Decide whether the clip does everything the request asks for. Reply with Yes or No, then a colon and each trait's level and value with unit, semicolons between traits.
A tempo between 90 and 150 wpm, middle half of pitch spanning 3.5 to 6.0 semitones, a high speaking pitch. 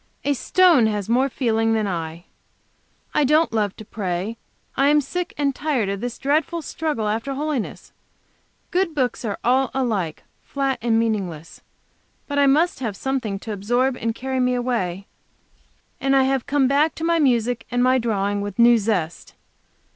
No: average, 170 wpm; average, 4.5 semitones; high, 245 Hz